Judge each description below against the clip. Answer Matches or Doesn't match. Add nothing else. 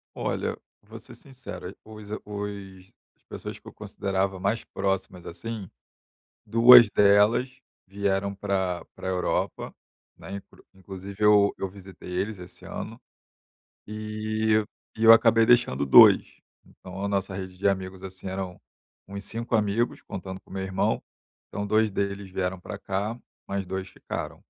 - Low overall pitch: Matches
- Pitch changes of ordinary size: Doesn't match